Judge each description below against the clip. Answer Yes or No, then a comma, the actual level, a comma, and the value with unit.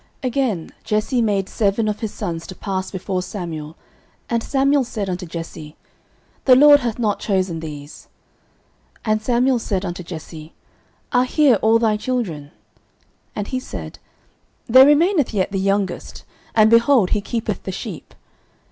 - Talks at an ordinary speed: Yes, average, 155 wpm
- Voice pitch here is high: Yes, high, 210 Hz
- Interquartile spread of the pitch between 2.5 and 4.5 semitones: No, average, 5.1 semitones